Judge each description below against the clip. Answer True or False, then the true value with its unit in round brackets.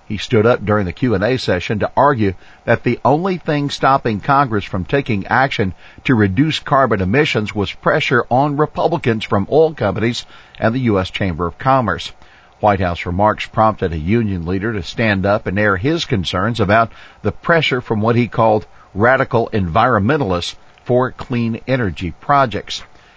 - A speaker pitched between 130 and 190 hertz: False (110 Hz)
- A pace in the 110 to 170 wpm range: True (160 wpm)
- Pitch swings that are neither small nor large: True (4.8 semitones)